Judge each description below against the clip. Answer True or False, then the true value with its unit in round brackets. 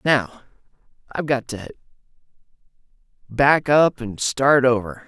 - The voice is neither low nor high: False (130 Hz)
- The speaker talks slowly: True (105 wpm)